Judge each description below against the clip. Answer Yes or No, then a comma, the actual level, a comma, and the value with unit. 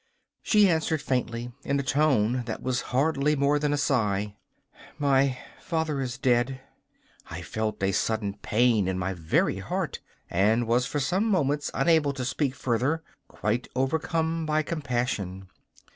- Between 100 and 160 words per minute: Yes, average, 145 wpm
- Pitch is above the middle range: No, low, 130 Hz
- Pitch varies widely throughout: No, average, 4.8 semitones